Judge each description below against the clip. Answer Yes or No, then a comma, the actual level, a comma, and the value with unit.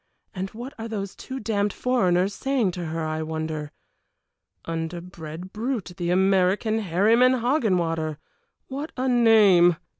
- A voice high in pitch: Yes, high, 195 Hz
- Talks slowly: Yes, slow, 125 wpm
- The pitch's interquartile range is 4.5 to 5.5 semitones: Yes, average, 5.2 semitones